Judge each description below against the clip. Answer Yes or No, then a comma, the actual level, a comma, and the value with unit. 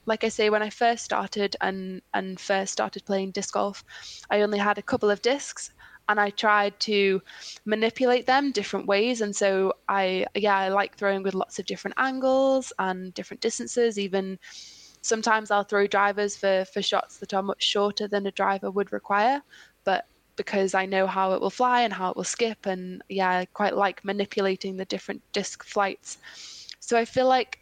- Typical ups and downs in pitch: No, narrow, 2.3 semitones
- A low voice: No, high, 205 Hz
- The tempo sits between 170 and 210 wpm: Yes, average, 190 wpm